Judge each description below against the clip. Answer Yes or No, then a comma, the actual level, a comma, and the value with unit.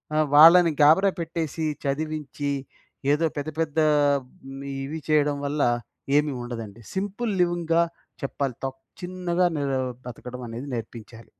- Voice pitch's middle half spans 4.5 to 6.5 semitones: No, average, 3.8 semitones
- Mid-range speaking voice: Yes, medium, 150 Hz